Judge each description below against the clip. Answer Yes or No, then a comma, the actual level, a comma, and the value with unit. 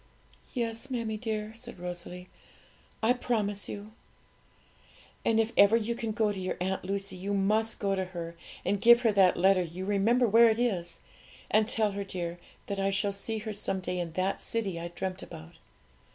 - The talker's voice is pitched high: Yes, high, 200 Hz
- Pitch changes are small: No, average, 3.3 semitones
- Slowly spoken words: No, average, 185 wpm